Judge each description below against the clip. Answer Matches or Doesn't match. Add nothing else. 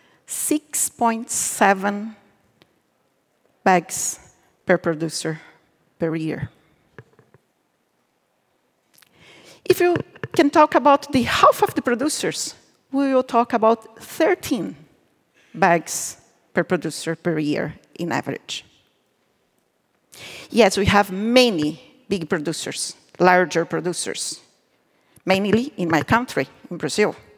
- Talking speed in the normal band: Doesn't match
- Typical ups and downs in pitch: Doesn't match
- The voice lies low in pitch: Doesn't match